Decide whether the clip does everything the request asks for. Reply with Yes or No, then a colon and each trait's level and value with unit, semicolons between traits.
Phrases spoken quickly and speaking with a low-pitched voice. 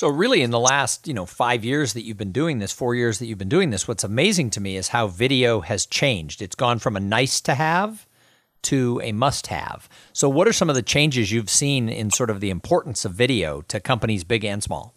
Yes: fast, 250 wpm; low, 120 Hz